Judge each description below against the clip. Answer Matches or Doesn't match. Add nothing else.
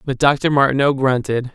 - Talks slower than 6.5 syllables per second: Matches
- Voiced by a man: Matches